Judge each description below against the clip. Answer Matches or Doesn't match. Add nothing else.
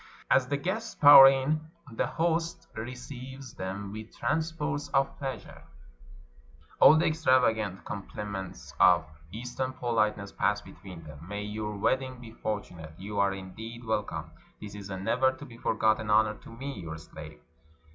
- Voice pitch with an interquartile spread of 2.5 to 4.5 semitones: Doesn't match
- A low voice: Matches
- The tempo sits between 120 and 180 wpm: Matches